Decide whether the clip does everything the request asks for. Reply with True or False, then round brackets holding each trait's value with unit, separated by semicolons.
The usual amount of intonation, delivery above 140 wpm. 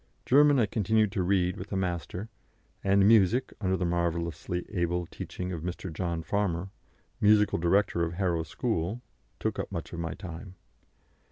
True (3.1 semitones; 160 wpm)